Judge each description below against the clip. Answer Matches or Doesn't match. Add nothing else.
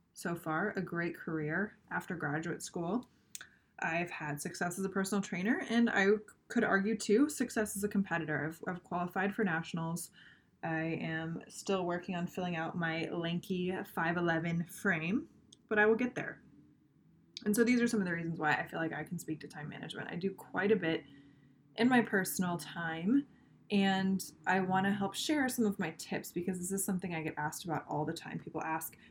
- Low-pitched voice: Doesn't match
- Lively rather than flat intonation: Doesn't match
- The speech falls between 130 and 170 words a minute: Doesn't match